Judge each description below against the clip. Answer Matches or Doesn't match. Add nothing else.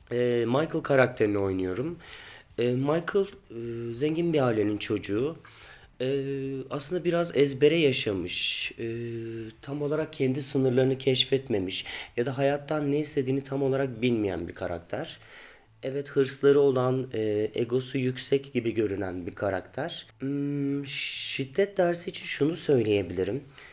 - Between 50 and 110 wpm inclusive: Matches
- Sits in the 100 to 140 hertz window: Matches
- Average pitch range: Matches